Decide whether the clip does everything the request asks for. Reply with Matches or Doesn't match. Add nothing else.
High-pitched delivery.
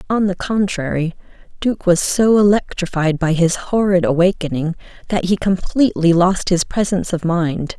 Doesn't match